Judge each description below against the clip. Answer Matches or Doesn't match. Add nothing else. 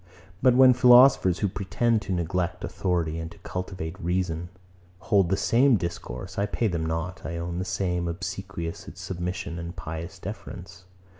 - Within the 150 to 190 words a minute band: Matches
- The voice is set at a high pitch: Doesn't match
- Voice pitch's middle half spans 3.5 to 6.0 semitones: Doesn't match